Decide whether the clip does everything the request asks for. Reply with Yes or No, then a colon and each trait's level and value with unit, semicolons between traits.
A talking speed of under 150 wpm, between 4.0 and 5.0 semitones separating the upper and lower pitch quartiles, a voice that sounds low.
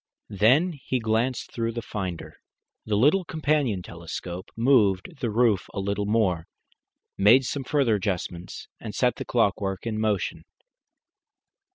Yes: slow, 135 wpm; average, 4.4 semitones; low, 110 Hz